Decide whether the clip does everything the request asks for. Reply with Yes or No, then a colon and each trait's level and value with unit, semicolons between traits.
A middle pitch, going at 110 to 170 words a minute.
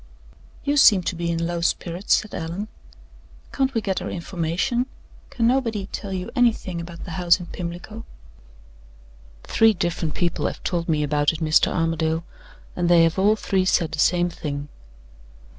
Yes: medium, 175 Hz; average, 165 wpm